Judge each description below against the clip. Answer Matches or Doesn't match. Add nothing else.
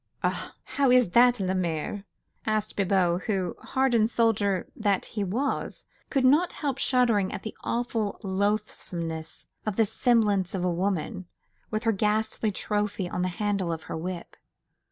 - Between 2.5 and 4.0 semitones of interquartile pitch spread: Matches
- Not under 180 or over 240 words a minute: Doesn't match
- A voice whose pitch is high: Matches